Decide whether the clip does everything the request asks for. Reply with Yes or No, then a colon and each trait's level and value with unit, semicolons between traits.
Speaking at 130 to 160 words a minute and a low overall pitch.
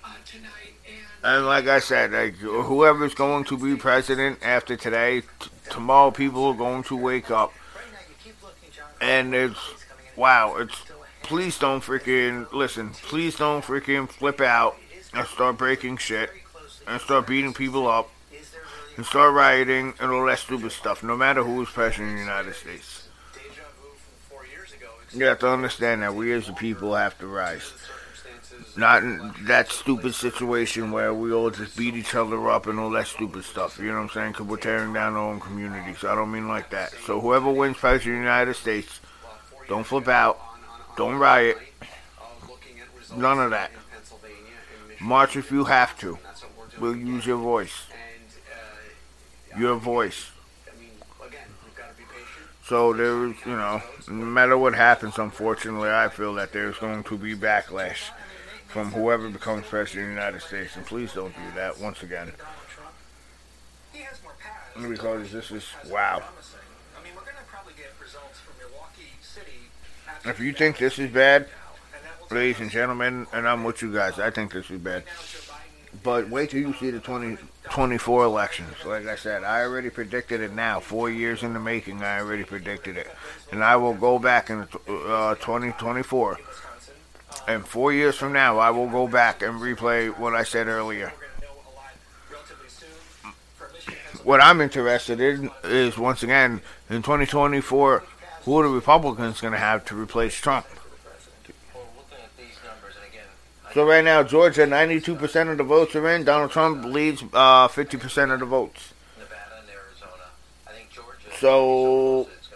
Yes: average, 150 wpm; low, 120 Hz